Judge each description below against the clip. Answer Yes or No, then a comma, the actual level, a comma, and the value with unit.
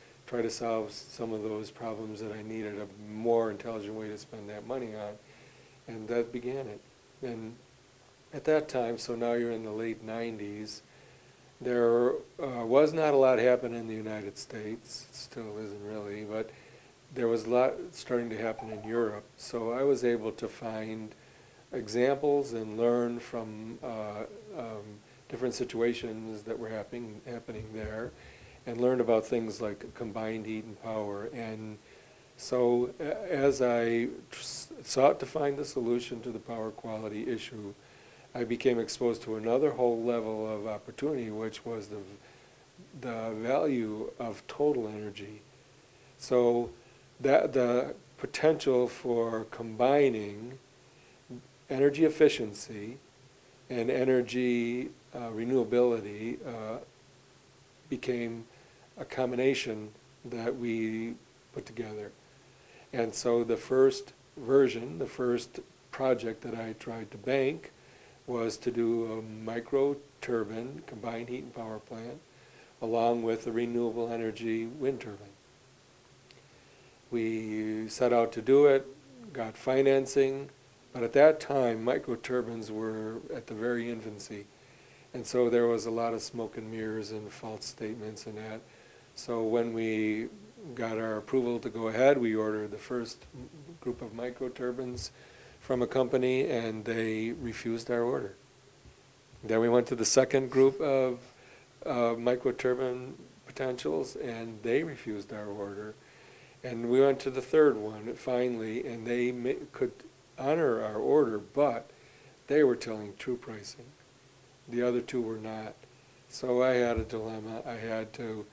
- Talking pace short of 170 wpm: Yes, average, 140 wpm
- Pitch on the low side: Yes, low, 115 Hz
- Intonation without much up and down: Yes, narrow, 2.3 semitones